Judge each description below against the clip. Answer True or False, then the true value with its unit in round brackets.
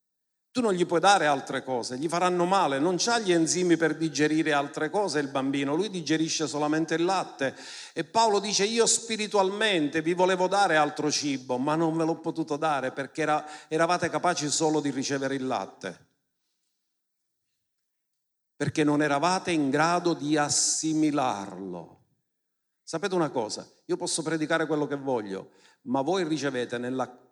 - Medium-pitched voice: True (155 Hz)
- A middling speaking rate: True (155 wpm)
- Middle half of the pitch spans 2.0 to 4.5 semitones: True (3.4 semitones)